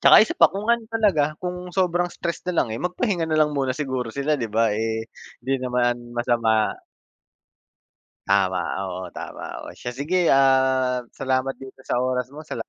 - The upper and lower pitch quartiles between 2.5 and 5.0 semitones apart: No, wide, 5.4 semitones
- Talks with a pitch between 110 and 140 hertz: Yes, low, 135 Hz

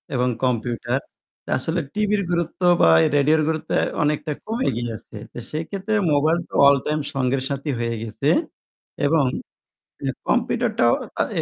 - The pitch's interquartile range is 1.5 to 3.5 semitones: No, average, 4.4 semitones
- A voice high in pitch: No, medium, 150 Hz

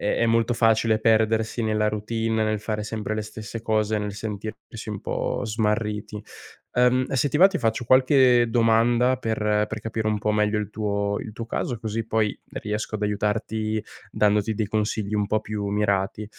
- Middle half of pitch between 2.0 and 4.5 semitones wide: No, narrow, 1.3 semitones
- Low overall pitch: Yes, low, 110 Hz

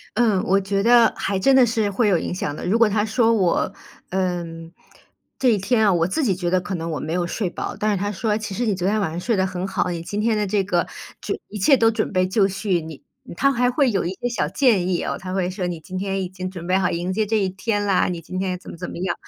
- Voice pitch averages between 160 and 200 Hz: Yes, high, 190 Hz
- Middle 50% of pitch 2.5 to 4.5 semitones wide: Yes, average, 3.2 semitones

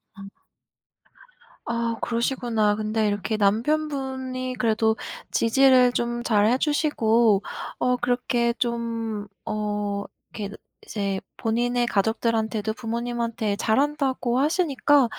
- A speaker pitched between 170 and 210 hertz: No, high, 235 Hz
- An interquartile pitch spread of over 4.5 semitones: No, narrow, 2.6 semitones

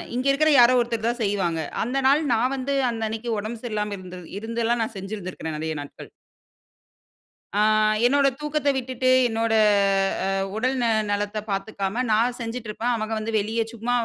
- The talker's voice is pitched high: Yes, high, 225 Hz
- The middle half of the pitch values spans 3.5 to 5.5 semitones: No, average, 3.1 semitones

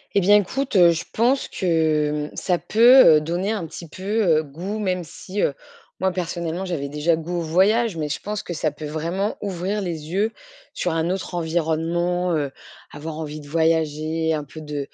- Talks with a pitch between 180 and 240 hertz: No, medium, 170 Hz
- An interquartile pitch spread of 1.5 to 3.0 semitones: No, average, 3.4 semitones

